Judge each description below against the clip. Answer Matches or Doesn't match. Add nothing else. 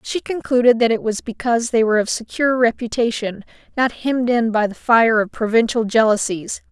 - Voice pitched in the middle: Doesn't match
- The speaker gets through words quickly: Doesn't match